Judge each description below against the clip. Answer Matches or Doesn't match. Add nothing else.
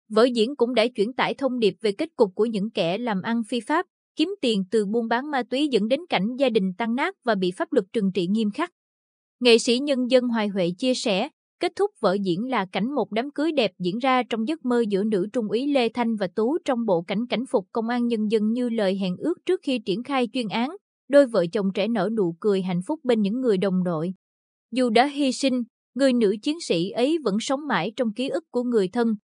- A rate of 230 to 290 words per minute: Matches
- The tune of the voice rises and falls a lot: Doesn't match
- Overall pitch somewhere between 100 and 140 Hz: Doesn't match